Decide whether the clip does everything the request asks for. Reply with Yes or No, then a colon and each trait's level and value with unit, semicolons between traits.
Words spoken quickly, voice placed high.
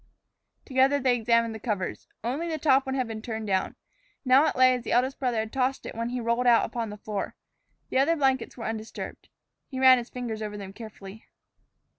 Yes: fast, 210 wpm; high, 240 Hz